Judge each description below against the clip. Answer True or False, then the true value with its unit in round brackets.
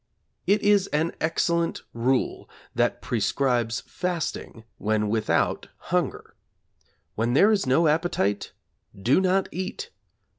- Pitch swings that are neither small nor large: False (7.9 semitones)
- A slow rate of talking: True (110 wpm)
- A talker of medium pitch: True (150 Hz)